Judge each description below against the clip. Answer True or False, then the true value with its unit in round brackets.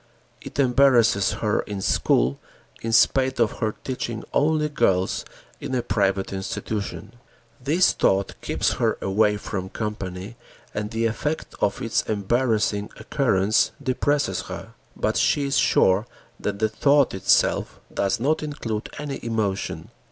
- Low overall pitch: True (110 Hz)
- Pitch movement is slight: False (4.7 semitones)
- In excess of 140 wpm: False (135 wpm)